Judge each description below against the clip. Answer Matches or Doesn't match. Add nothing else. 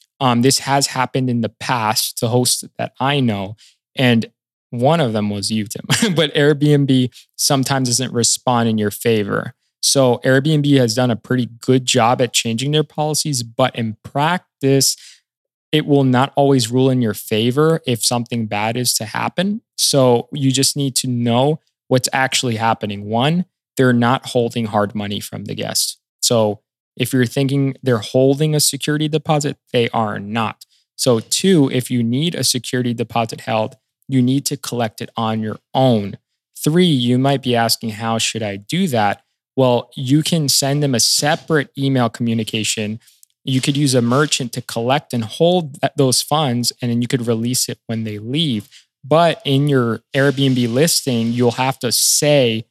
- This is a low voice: Matches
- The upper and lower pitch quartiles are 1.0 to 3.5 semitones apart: Matches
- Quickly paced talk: Doesn't match